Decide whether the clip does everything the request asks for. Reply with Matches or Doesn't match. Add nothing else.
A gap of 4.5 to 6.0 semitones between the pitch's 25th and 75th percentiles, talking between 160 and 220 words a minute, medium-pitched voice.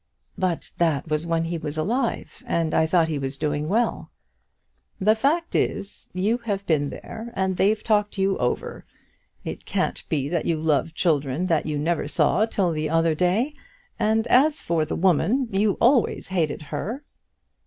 Matches